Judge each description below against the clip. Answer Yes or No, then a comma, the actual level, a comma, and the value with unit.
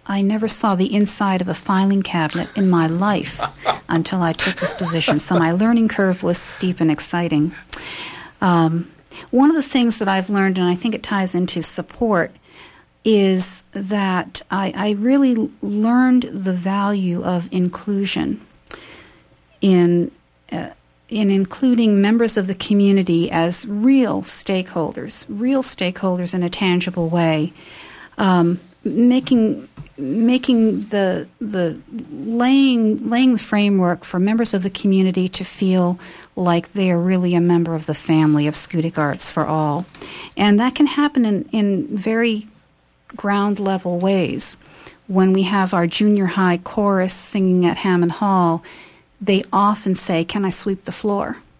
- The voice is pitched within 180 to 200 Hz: Yes, high, 190 Hz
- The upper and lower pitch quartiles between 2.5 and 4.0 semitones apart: Yes, average, 3.3 semitones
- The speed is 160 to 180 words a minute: No, average, 150 wpm